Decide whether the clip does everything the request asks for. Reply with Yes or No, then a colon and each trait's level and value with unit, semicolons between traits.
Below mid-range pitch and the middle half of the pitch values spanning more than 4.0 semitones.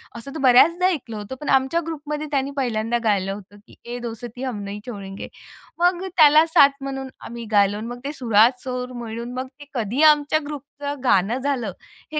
No: very high, 255 Hz; average, 4.4 semitones